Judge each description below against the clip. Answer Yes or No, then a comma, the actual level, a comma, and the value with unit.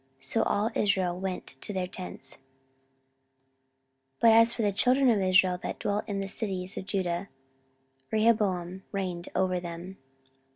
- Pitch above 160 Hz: Yes, high, 190 Hz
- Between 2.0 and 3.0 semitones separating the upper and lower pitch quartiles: Yes, narrow, 2.6 semitones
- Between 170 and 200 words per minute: No, average, 150 wpm